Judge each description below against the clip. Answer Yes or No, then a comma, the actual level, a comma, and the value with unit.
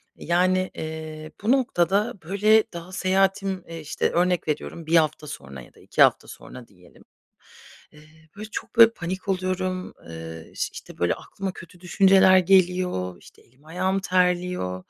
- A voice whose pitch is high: No, medium, 180 Hz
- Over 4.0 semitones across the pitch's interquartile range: No, average, 3.4 semitones